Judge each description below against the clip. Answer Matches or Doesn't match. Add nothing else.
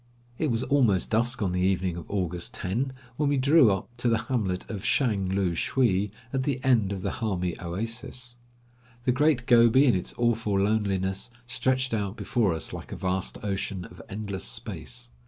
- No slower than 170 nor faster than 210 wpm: Matches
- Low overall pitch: Matches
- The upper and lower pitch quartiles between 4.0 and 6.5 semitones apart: Matches